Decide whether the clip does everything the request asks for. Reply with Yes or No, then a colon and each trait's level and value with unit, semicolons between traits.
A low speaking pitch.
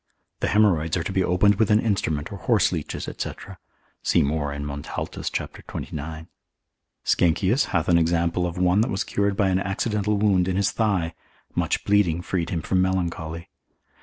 Yes: very low, 90 Hz